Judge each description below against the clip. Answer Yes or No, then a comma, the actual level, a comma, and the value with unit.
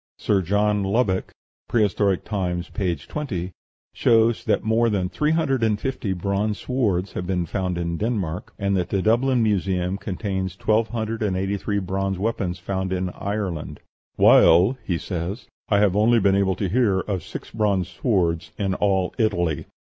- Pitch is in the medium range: No, low, 100 Hz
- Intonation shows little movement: No, average, 3.0 semitones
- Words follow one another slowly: No, average, 165 wpm